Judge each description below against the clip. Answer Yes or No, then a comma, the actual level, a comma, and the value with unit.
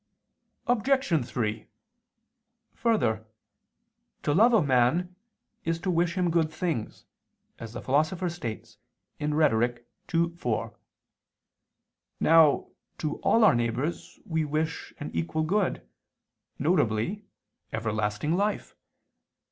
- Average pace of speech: No, slow, 100 wpm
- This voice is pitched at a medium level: Yes, medium, 155 Hz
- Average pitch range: No, wide, 6.8 semitones